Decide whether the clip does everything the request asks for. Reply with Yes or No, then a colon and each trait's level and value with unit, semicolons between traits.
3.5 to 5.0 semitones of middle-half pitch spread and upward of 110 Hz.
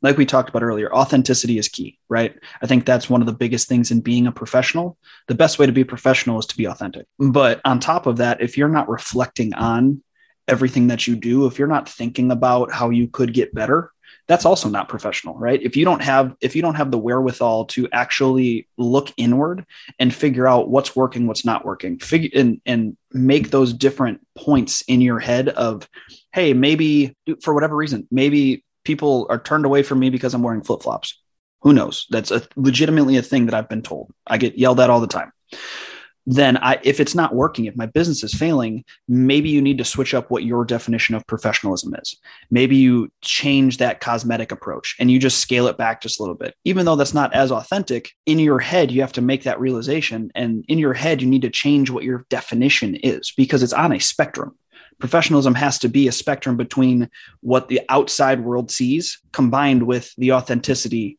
No: narrow, 2.5 semitones; low, 130 Hz